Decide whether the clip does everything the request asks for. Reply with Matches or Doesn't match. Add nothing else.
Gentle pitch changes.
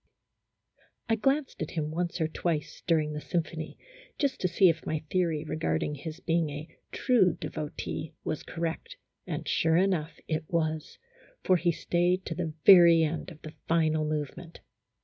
Matches